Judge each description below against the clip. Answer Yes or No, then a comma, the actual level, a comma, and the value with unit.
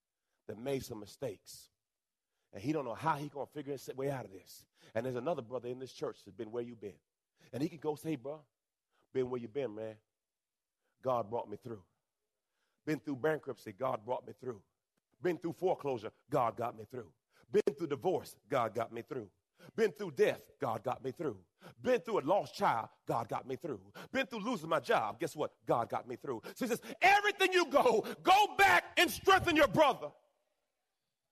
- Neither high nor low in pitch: Yes, medium, 150 Hz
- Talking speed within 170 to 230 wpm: Yes, average, 200 wpm